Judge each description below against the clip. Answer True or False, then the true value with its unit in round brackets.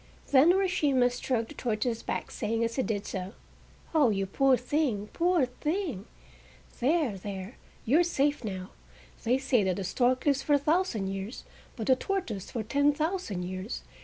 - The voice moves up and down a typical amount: False (6.0 semitones)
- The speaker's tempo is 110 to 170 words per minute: True (165 wpm)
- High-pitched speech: True (250 Hz)